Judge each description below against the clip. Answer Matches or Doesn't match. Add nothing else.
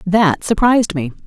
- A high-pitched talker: Matches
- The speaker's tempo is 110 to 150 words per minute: Matches